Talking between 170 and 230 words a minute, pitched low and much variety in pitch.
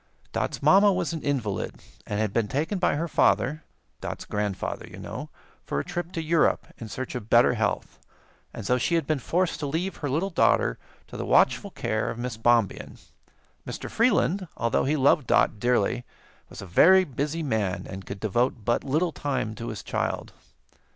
Yes: average, 185 wpm; low, 130 Hz; wide, 7.0 semitones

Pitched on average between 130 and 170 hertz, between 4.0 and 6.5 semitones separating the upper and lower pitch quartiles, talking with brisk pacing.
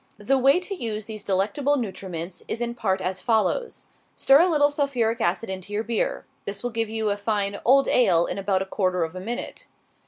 No: high, 220 Hz; average, 4.5 semitones; fast, 210 wpm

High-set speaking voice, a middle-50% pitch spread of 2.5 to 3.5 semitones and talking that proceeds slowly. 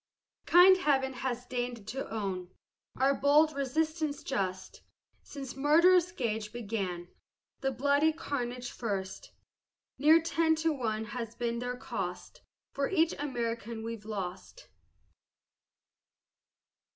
No: very high, 255 Hz; average, 5.2 semitones; slow, 110 wpm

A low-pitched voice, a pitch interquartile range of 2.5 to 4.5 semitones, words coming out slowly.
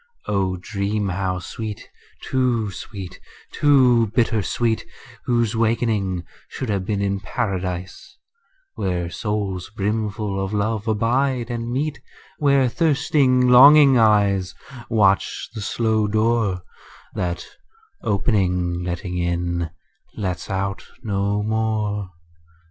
Yes: low, 105 Hz; average, 3.5 semitones; slow, 105 wpm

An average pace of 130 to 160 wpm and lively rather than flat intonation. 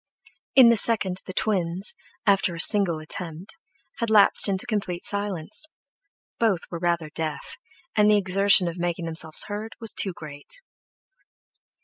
No: average, 140 wpm; average, 3.7 semitones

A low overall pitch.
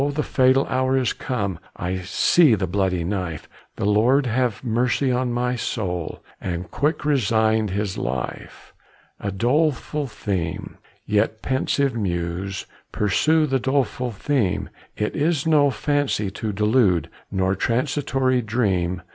Yes: low, 110 Hz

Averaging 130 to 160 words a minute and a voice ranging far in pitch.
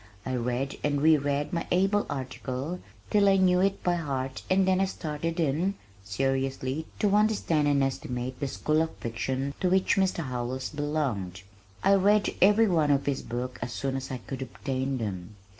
No: average, 180 wpm; wide, 5.7 semitones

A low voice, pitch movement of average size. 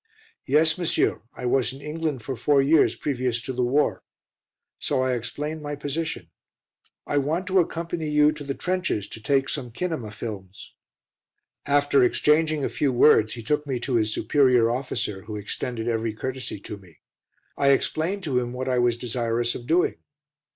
Yes: low, 130 Hz; average, 3.9 semitones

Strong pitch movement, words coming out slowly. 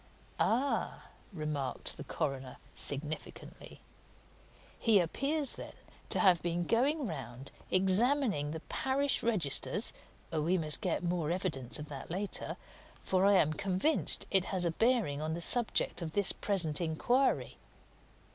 Yes: wide, 6.4 semitones; slow, 130 wpm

